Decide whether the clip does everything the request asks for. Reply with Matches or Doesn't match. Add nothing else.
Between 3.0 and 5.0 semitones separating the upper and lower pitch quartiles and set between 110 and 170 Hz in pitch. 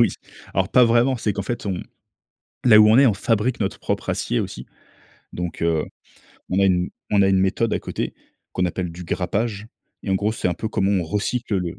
Doesn't match